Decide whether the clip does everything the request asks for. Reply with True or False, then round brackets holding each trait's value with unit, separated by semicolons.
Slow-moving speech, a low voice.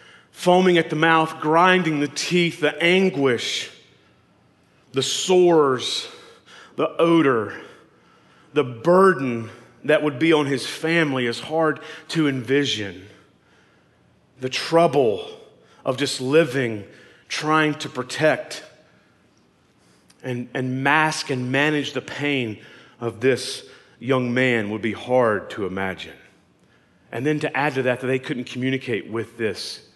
False (120 wpm; 145 Hz)